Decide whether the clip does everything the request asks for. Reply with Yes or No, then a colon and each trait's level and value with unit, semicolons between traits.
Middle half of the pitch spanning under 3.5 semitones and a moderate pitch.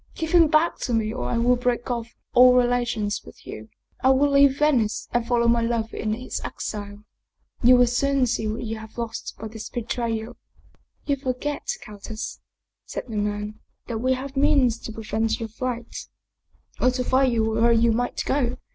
No: narrow, 2.5 semitones; high, 235 Hz